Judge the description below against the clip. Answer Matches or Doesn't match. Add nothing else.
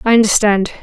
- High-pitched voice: Matches